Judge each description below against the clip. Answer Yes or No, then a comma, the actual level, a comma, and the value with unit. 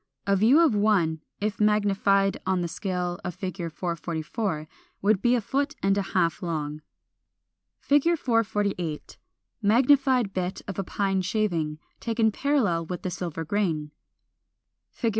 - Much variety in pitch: No, average, 4.0 semitones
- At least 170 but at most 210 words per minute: No, average, 140 wpm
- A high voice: Yes, high, 195 Hz